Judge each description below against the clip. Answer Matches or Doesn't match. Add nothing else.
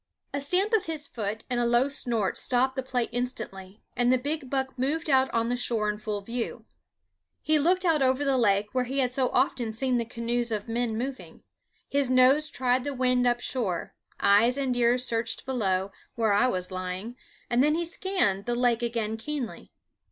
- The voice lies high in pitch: Matches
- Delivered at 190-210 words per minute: Matches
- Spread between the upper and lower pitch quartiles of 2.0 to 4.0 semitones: Matches